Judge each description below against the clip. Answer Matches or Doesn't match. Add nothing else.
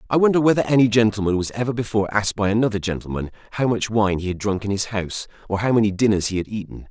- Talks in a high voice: Doesn't match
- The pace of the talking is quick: Matches